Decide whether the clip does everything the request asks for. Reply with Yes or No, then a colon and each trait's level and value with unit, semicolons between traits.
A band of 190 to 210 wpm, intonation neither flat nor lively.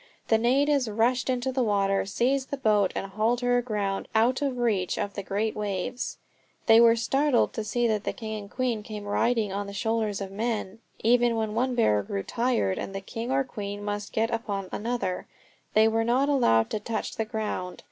Yes: average, 200 wpm; average, 3.1 semitones